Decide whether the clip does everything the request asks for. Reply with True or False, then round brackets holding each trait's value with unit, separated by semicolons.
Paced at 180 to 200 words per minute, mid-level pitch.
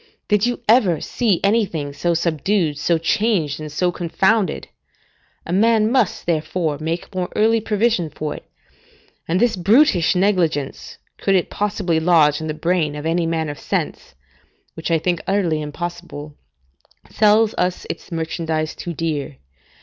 False (150 wpm; 175 Hz)